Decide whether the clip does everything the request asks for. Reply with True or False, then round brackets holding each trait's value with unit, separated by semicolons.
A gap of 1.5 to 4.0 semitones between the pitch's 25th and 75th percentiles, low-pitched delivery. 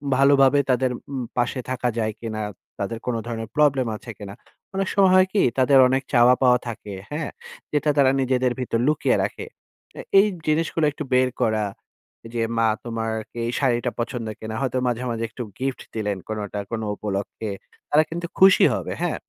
True (3.5 semitones; 125 Hz)